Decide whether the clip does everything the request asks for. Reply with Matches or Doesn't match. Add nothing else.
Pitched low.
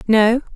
Doesn't match